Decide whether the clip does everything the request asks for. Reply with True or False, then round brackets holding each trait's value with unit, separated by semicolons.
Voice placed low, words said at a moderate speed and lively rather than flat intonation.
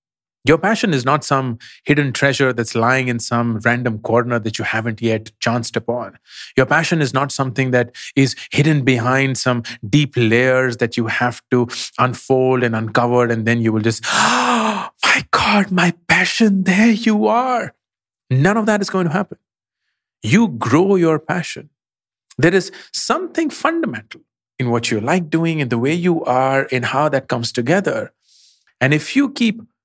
True (130 Hz; 170 wpm; 5.9 semitones)